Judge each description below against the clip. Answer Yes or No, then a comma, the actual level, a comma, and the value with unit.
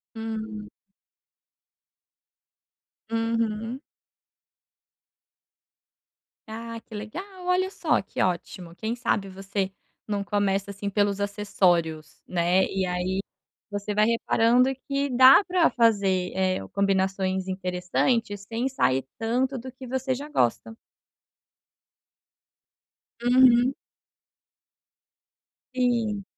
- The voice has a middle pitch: No, high, 210 Hz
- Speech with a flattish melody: No, average, 4.1 semitones